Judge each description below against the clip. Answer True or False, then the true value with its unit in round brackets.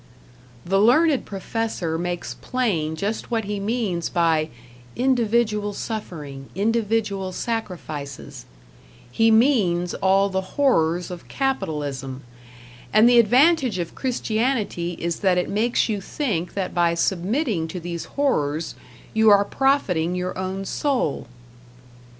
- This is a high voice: True (195 Hz)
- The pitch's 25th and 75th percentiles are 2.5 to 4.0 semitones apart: False (5.1 semitones)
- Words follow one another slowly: True (120 wpm)